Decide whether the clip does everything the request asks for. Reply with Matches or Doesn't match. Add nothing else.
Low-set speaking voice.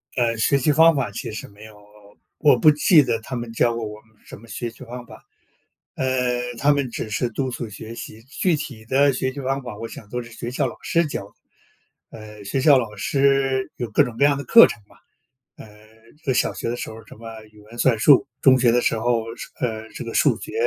Matches